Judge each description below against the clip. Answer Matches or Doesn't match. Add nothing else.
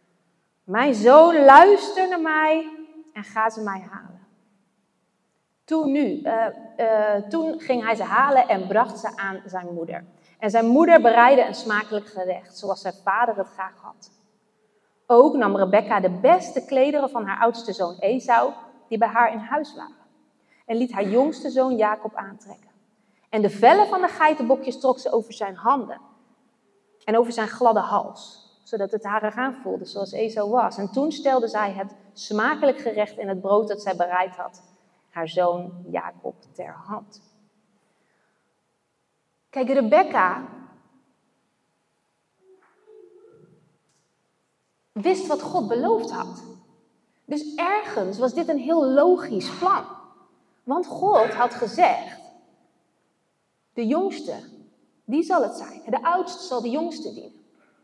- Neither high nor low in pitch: Doesn't match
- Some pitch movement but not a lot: Doesn't match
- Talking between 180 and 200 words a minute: Doesn't match